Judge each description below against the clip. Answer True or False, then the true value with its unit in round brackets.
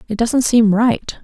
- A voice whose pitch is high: True (225 Hz)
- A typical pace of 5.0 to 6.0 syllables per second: False (3.9 syllables/s)